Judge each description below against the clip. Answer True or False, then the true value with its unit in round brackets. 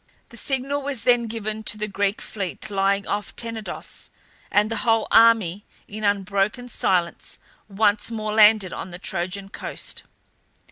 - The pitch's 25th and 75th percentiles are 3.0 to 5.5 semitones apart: False (2.4 semitones)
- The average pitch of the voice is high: True (210 Hz)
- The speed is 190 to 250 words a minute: False (145 wpm)